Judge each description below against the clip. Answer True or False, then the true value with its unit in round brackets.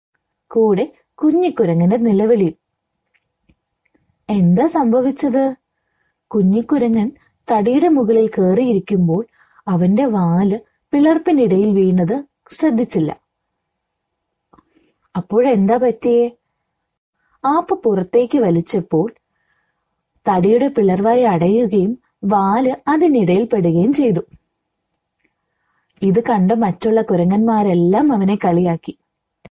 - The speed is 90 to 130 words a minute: False (65 wpm)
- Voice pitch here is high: True (215 Hz)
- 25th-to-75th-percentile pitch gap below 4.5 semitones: False (5.2 semitones)